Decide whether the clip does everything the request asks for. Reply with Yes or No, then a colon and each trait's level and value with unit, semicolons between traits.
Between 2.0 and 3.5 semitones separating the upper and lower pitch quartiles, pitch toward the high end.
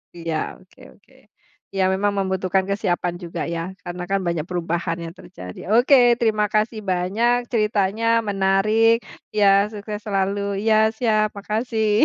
Yes: average, 3.1 semitones; high, 200 Hz